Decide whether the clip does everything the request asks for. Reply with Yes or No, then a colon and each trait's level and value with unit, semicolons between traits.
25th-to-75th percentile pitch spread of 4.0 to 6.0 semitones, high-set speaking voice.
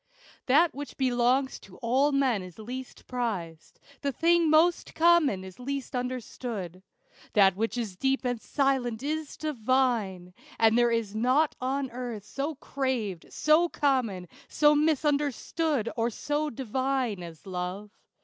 Yes: average, 4.7 semitones; very high, 250 Hz